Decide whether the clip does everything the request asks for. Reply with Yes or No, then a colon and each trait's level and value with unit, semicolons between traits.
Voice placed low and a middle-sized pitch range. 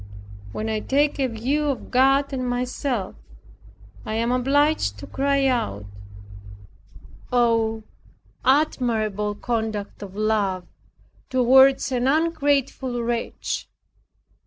No: high, 245 Hz; average, 3.8 semitones